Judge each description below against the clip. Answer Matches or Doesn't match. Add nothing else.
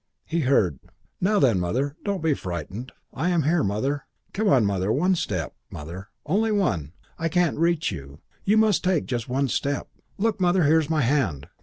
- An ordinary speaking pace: Matches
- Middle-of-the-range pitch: Matches